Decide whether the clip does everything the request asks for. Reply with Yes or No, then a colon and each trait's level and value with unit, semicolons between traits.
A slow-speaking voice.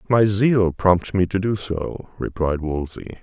No: average, 165 wpm